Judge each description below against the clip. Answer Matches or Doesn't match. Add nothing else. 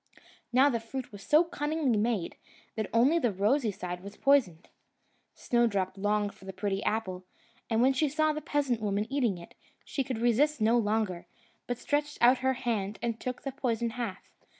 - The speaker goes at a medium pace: Matches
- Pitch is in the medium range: Doesn't match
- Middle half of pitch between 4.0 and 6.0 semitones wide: Matches